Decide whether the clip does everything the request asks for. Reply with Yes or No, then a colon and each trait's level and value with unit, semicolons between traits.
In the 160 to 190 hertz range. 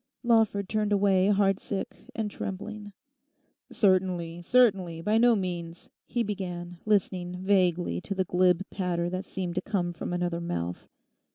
Yes: medium, 185 Hz